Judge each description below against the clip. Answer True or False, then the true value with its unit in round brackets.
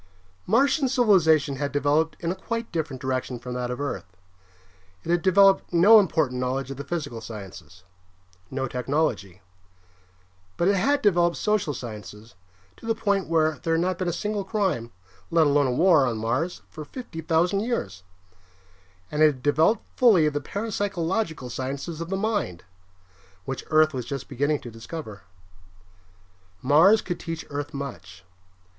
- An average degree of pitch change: False (6.5 semitones)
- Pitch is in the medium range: True (155 Hz)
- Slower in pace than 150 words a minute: False (155 wpm)